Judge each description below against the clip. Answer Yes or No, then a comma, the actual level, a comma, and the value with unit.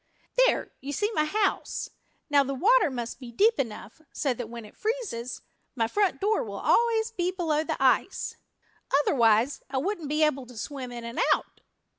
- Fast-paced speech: No, average, 180 wpm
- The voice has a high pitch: Yes, very high, 290 Hz